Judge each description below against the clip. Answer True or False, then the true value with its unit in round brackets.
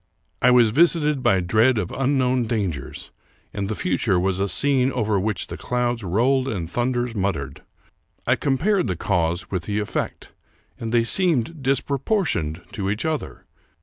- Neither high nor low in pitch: False (115 Hz)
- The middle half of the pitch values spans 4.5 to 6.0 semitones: True (5.4 semitones)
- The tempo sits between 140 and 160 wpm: True (155 wpm)